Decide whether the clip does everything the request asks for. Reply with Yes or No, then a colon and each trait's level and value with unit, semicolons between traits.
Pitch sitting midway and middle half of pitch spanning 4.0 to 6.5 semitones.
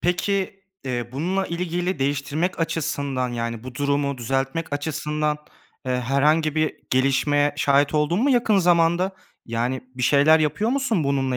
Yes: medium, 145 Hz; average, 4.3 semitones